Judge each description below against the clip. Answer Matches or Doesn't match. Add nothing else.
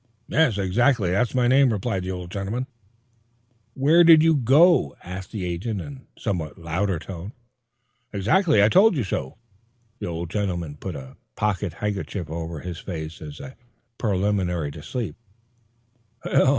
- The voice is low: Matches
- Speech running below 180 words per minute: Matches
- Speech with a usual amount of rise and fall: Doesn't match